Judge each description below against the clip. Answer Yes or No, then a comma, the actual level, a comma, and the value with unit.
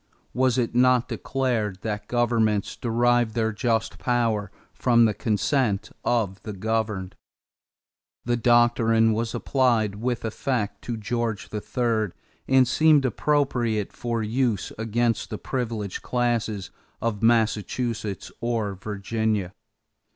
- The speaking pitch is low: Yes, low, 115 Hz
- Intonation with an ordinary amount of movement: No, narrow, 2.3 semitones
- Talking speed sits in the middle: No, slow, 115 wpm